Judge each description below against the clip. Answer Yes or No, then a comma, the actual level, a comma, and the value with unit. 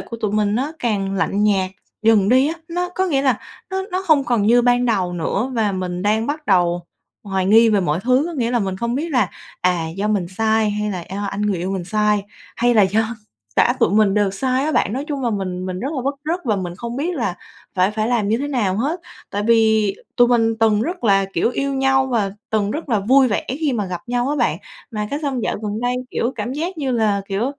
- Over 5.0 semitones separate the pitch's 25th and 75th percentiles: No, average, 4.5 semitones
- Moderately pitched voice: No, high, 220 Hz